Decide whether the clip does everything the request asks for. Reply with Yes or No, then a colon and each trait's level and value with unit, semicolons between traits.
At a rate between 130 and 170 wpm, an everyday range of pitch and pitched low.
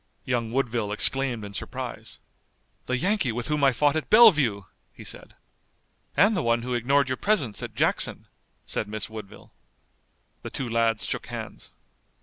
Yes: average, 155 wpm; average, 4.1 semitones; low, 125 Hz